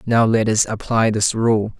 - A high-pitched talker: No, low, 110 Hz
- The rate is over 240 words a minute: No, average, 200 wpm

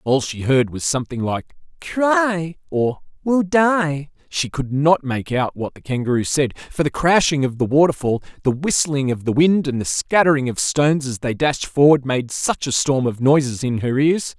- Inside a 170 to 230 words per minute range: Yes, average, 200 wpm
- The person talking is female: No, male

